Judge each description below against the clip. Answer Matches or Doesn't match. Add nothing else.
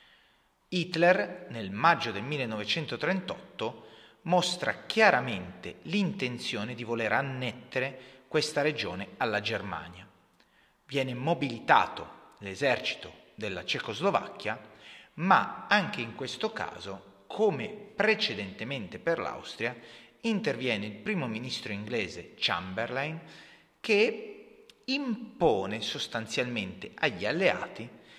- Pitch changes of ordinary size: Doesn't match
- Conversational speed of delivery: Doesn't match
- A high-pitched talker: Doesn't match